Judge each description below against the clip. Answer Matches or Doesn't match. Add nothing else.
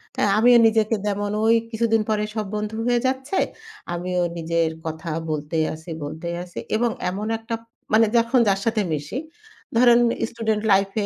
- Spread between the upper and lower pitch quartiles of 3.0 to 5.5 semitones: Matches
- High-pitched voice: Matches